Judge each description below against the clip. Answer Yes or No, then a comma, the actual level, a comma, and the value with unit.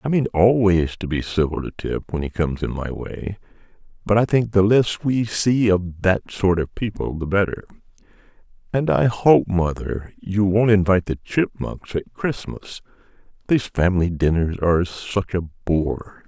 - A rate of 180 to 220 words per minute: No, average, 165 wpm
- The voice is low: Yes, very low, 95 Hz